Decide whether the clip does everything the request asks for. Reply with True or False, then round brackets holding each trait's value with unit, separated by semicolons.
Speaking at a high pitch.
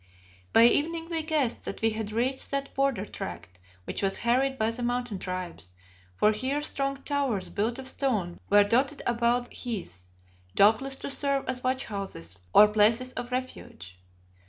True (240 Hz)